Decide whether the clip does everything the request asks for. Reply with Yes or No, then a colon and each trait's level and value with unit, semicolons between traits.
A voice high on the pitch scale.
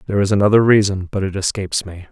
No: very low, 95 Hz